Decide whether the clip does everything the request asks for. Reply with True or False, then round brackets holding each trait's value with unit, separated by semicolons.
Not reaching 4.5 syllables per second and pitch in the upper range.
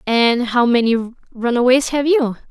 True (4.0 syllables/s; 245 Hz)